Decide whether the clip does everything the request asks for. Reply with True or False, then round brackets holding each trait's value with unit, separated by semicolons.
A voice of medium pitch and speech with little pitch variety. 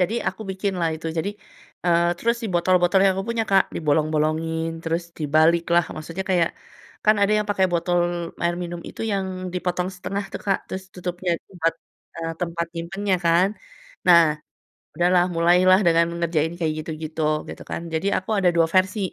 True (175 Hz; 2.2 semitones)